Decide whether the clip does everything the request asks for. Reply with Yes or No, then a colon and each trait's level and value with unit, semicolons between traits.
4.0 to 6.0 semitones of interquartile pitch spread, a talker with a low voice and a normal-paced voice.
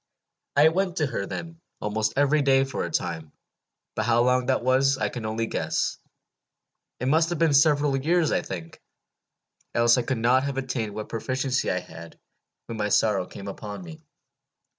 Yes: average, 4.6 semitones; low, 125 Hz; average, 180 wpm